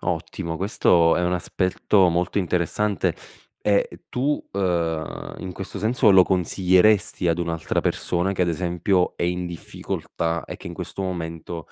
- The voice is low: Yes, very low, 90 Hz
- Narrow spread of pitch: Yes, narrow, 2.1 semitones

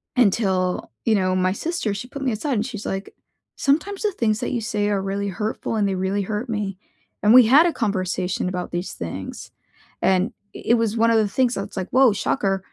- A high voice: Yes, high, 210 Hz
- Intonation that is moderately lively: Yes, average, 3.8 semitones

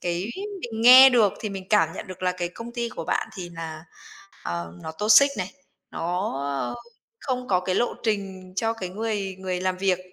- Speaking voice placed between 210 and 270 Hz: No, high, 190 Hz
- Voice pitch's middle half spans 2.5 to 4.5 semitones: Yes, average, 3.9 semitones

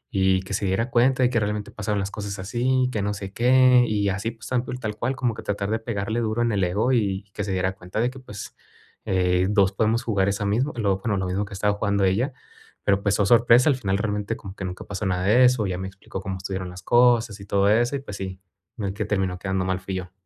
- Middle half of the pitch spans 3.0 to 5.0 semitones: Yes, average, 3.4 semitones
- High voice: No, low, 105 Hz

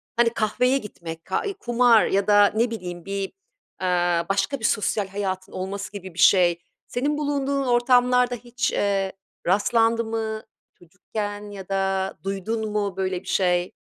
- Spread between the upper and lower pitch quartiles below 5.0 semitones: Yes, average, 3.6 semitones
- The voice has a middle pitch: No, high, 205 Hz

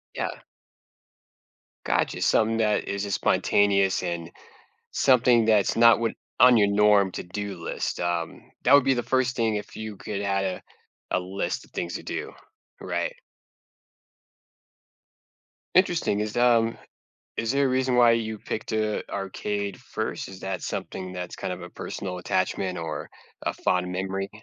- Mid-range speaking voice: No, low, 105 Hz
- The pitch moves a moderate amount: Yes, average, 3.2 semitones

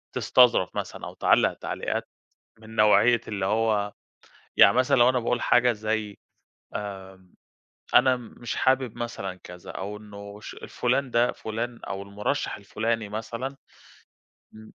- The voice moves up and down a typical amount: Yes, average, 3.1 semitones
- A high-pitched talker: No, low, 110 Hz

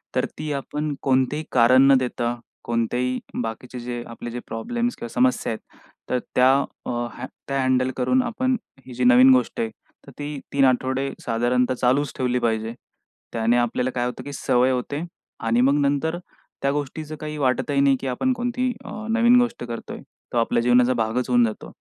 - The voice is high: No, low, 130 Hz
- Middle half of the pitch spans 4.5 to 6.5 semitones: No, average, 3.0 semitones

